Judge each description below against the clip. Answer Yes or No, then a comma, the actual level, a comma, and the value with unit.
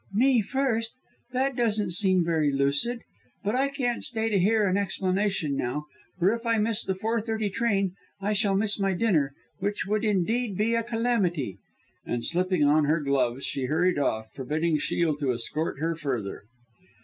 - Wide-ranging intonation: Yes, wide, 6.7 semitones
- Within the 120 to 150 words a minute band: No, average, 175 wpm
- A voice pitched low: No, high, 195 Hz